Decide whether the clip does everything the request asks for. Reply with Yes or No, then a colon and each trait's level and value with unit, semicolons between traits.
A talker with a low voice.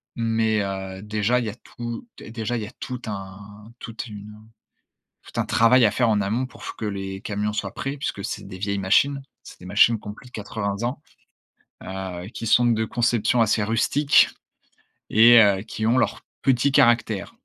Yes: low, 110 Hz